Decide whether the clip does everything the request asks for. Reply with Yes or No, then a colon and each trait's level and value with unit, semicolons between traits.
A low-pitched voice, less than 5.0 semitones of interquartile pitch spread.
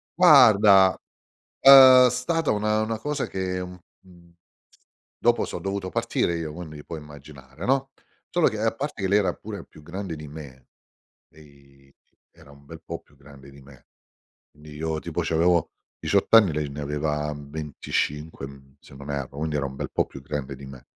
No: very low, 80 Hz; wide, 5.7 semitones